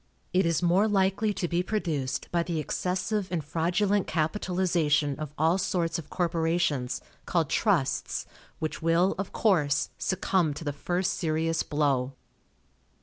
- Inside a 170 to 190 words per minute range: No, average, 140 wpm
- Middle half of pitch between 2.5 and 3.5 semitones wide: Yes, average, 3.1 semitones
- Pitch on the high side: No, medium, 170 Hz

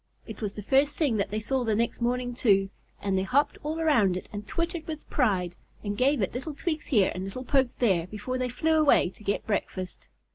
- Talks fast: Yes, fast, 225 wpm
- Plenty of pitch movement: Yes, wide, 6.0 semitones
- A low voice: No, high, 240 Hz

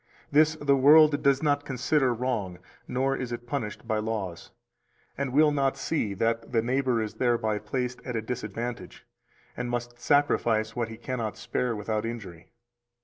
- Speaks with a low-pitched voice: Yes, low, 120 Hz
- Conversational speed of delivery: Yes, average, 160 wpm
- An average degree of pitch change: Yes, average, 3.5 semitones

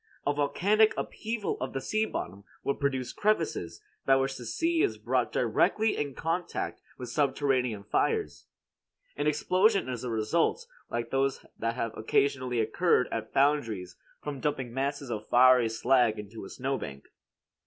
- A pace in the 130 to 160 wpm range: Yes, average, 150 wpm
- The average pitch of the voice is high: No, low, 135 Hz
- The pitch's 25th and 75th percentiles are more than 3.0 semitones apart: Yes, average, 4.4 semitones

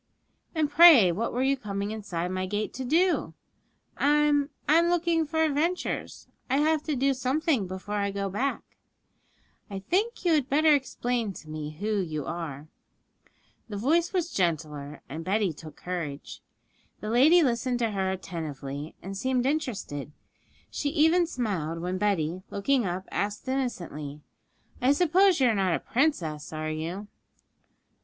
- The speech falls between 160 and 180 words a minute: No, average, 150 wpm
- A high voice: Yes, high, 215 Hz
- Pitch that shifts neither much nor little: No, wide, 8.7 semitones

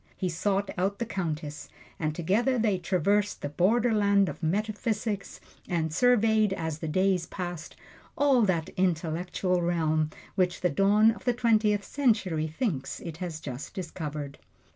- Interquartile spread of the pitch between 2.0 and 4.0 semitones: No, average, 4.6 semitones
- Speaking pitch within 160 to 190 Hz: Yes, medium, 185 Hz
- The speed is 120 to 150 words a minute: Yes, average, 145 wpm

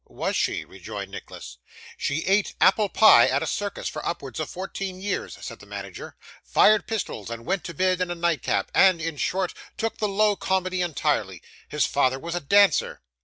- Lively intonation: No, average, 4.3 semitones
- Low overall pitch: No, medium, 185 Hz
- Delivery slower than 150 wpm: No, average, 185 wpm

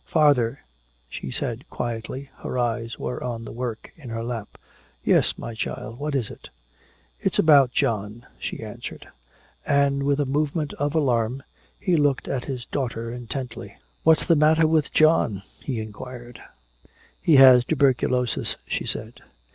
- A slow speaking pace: No, average, 145 wpm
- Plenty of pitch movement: No, average, 3.7 semitones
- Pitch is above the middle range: No, low, 125 Hz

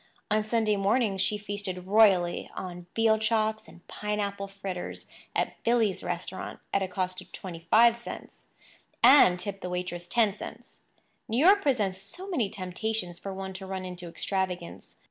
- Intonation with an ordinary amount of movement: Yes, average, 3.1 semitones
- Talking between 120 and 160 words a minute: Yes, average, 155 wpm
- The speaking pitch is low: No, high, 195 Hz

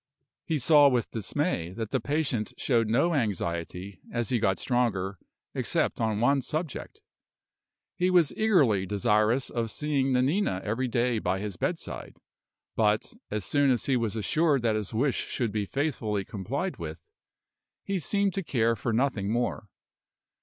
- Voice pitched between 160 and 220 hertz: No, low, 120 Hz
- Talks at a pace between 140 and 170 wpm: Yes, average, 155 wpm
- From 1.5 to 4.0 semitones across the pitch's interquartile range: No, average, 5.1 semitones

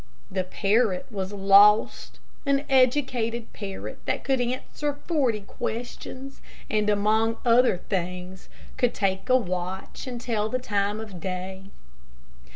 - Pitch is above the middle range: Yes, high, 215 Hz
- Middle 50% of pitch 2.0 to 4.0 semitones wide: No, average, 4.4 semitones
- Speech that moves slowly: Yes, slow, 125 wpm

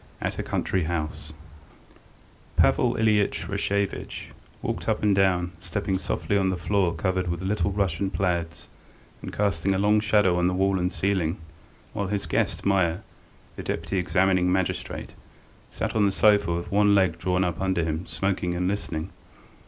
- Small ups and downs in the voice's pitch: Yes, narrow, 2.3 semitones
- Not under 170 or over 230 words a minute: No, average, 160 wpm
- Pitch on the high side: No, very low, 95 Hz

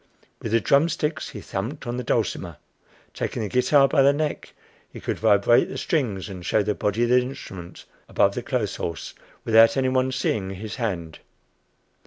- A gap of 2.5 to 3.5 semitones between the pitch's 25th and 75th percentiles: No, average, 4.6 semitones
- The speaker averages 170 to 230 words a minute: Yes, average, 180 wpm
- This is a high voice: No, low, 115 Hz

